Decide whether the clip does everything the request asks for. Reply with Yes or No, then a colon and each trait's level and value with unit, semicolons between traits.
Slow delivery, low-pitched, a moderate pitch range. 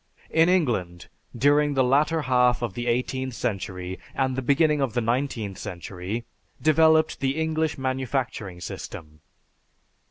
Yes: slow, 130 wpm; low, 130 Hz; average, 4.7 semitones